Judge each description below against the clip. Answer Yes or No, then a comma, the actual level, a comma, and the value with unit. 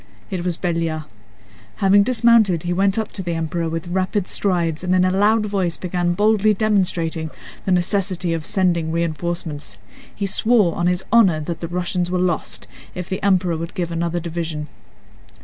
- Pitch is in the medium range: Yes, medium, 180 Hz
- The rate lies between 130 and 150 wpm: No, average, 170 wpm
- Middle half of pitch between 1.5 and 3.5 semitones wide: Yes, narrow, 2.6 semitones